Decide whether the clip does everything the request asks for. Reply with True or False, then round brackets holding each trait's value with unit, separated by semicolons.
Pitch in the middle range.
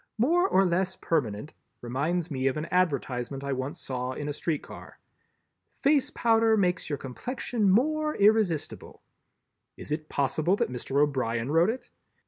True (160 Hz)